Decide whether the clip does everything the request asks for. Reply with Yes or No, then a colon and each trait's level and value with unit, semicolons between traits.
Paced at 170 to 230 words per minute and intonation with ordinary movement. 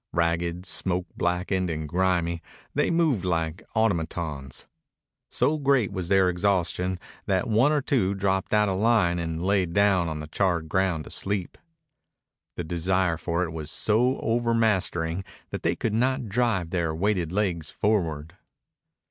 No: average, 150 wpm; average, 3.7 semitones